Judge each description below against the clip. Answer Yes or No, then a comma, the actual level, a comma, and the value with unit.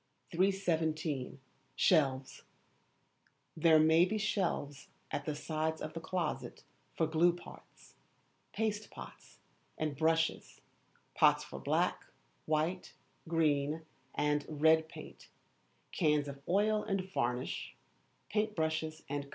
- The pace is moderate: No, slow, 110 wpm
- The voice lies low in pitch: No, medium, 160 Hz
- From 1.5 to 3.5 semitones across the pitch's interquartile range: Yes, average, 2.7 semitones